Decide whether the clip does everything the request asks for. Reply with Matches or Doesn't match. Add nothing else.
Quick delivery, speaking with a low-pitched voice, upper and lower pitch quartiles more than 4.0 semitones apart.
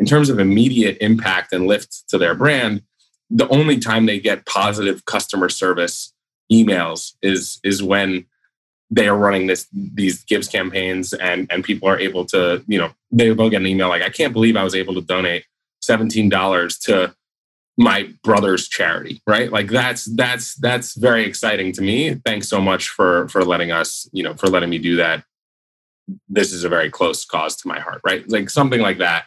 Doesn't match